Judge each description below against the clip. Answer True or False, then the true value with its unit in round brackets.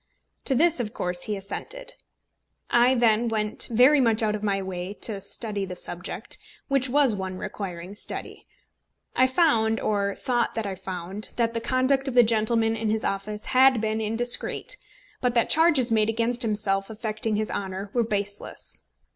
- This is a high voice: True (220 Hz)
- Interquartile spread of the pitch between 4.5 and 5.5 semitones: False (3.3 semitones)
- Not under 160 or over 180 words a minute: True (170 wpm)